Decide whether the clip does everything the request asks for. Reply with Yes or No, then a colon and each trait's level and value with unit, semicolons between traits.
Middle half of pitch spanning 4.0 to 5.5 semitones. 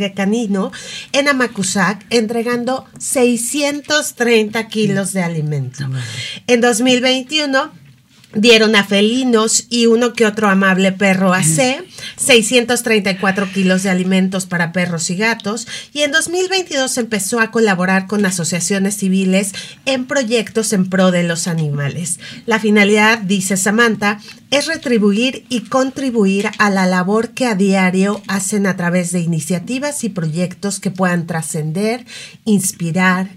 Yes: average, 4.3 semitones